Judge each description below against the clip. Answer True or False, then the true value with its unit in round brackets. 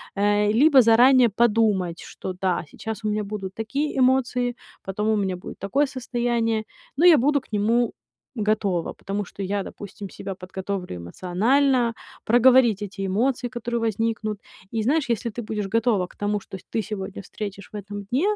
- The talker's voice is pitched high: True (215 Hz)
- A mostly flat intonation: False (3.4 semitones)